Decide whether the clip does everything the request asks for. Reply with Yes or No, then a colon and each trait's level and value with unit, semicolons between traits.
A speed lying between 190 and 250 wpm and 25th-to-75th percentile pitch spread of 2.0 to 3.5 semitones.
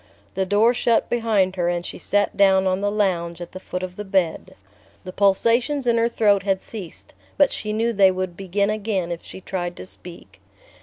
Yes: fast, 205 wpm; average, 2.7 semitones